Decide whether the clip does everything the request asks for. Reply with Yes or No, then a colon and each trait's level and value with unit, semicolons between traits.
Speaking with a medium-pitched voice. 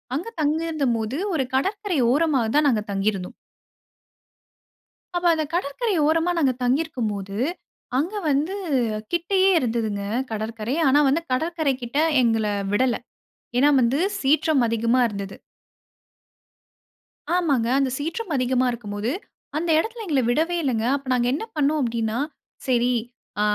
No: very high, 270 Hz